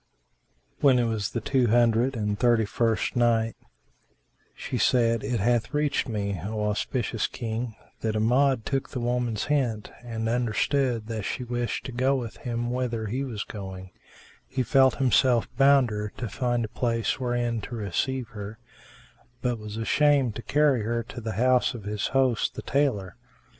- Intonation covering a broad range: No, narrow, 2.6 semitones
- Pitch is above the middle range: No, low, 120 Hz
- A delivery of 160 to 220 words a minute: Yes, average, 165 wpm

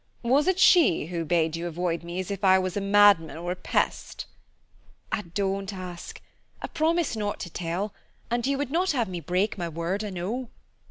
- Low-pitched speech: No, high, 190 Hz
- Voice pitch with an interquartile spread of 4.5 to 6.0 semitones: Yes, average, 5.1 semitones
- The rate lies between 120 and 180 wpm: No, average, 200 wpm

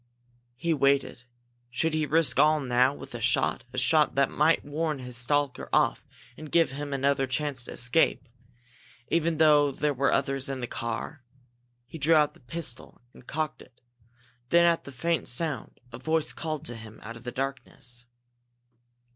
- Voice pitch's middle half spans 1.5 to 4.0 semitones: Yes, average, 3.7 semitones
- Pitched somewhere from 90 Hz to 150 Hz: Yes, medium, 140 Hz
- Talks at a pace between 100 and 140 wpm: No, average, 170 wpm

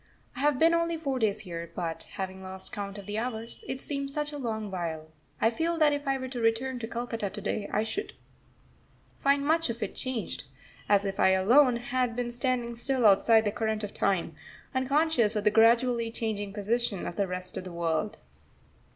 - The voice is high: Yes, high, 225 Hz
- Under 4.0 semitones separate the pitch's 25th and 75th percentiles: No, average, 4.6 semitones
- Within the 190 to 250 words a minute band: Yes, fast, 205 wpm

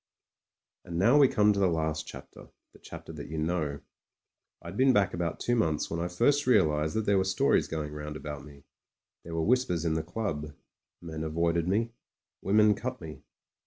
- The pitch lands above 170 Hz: No, very low, 85 Hz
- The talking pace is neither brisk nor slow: Yes, average, 195 wpm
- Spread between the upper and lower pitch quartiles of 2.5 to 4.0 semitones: No, average, 5.1 semitones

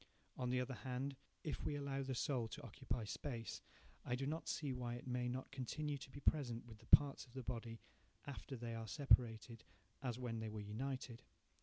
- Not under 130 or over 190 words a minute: No, average, 200 wpm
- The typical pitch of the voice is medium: No, low, 125 Hz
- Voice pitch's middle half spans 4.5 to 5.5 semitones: No, average, 2.8 semitones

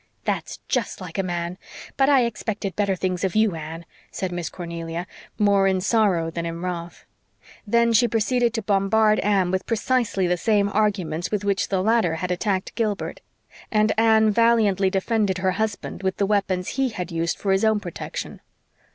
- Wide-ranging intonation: No, average, 3.3 semitones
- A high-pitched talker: Yes, high, 195 Hz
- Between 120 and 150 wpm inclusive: No, average, 175 wpm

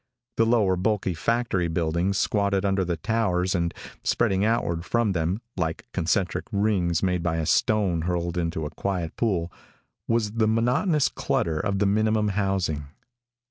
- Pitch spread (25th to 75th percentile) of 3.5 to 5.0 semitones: Yes, average, 4.1 semitones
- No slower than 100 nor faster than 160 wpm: Yes, average, 150 wpm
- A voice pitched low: Yes, very low, 95 Hz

